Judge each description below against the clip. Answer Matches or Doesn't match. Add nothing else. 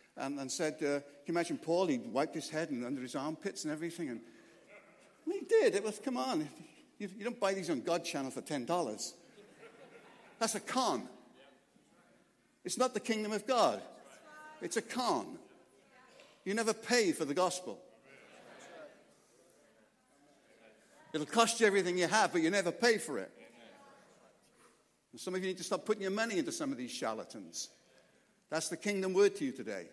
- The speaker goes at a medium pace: Matches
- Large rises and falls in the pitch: Matches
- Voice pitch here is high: Matches